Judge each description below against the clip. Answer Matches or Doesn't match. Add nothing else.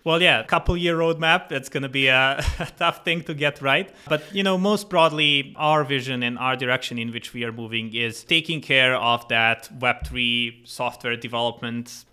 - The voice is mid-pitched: Doesn't match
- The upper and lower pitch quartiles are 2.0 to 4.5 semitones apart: Doesn't match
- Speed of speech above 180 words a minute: Matches